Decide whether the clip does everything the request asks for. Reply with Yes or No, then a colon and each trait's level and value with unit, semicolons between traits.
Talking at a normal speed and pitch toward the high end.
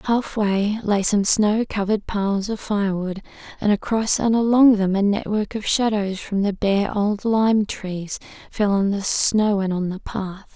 Yes: average, 175 wpm; high, 205 Hz